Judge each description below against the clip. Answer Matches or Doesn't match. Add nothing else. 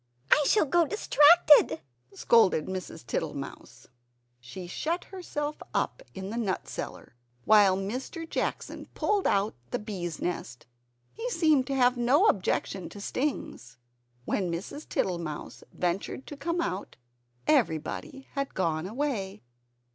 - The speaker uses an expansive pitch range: Matches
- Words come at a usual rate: Doesn't match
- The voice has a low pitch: Doesn't match